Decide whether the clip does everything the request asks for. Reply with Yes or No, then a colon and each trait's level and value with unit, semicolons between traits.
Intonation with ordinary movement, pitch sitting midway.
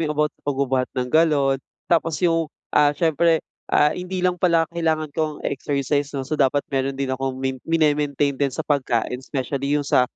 Yes: average, 3.0 semitones; medium, 145 Hz